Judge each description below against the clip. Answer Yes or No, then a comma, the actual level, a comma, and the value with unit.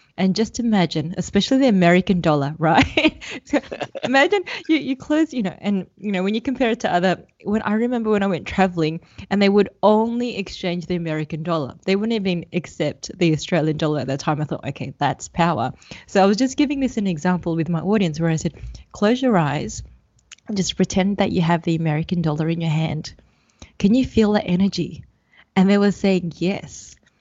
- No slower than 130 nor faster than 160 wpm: No, fast, 205 wpm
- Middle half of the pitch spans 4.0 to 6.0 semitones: Yes, average, 4.5 semitones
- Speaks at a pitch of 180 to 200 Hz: Yes, medium, 185 Hz